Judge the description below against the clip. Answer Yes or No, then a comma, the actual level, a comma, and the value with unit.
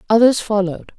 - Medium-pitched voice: No, high, 210 Hz